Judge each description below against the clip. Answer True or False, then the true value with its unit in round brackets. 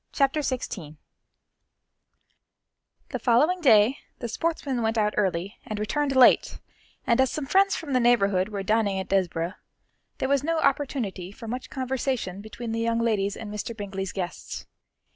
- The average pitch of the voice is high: True (230 Hz)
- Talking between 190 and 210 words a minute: False (155 wpm)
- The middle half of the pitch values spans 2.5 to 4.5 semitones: False (4.9 semitones)